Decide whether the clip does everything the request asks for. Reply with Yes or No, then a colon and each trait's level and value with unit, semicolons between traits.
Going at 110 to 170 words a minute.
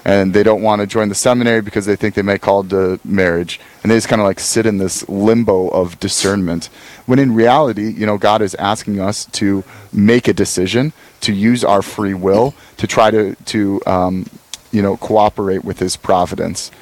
No: fast, 205 wpm